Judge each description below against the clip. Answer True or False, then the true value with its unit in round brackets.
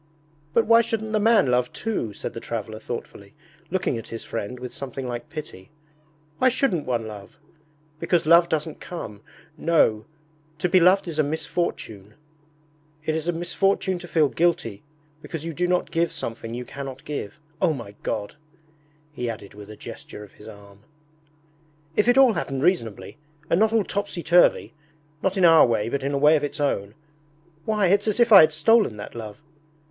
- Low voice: False (150 Hz)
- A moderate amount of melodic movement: False (7.7 semitones)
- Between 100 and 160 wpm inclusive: False (185 wpm)